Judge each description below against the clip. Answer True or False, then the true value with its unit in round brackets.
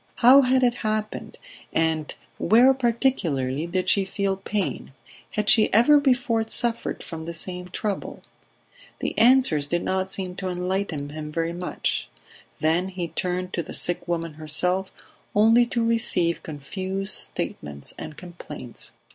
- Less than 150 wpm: True (140 wpm)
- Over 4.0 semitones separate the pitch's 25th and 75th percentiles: True (5.4 semitones)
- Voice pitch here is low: False (185 Hz)